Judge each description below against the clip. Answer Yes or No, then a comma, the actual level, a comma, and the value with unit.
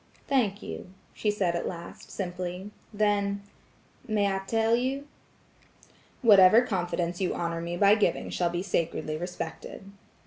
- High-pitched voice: Yes, high, 195 Hz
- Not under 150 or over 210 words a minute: No, slow, 135 wpm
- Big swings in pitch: No, average, 3.1 semitones